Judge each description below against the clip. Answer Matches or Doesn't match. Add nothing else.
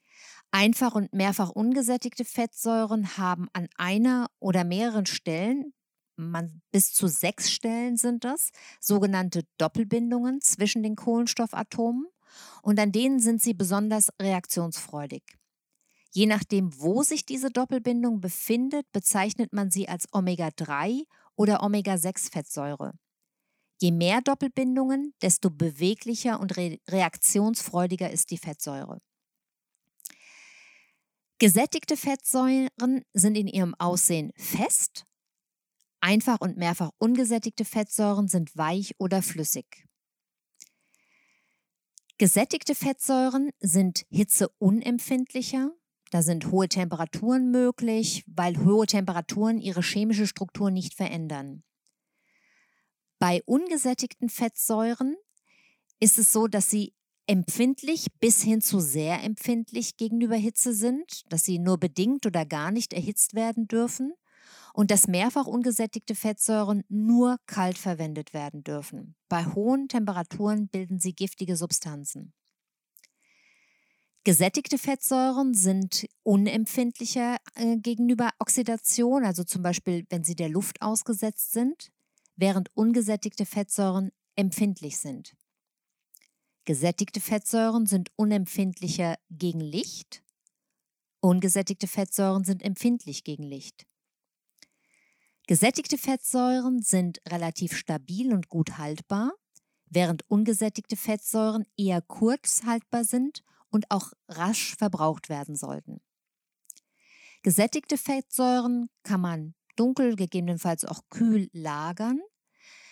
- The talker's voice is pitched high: Matches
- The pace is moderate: Doesn't match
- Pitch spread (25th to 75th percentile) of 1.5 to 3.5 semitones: Doesn't match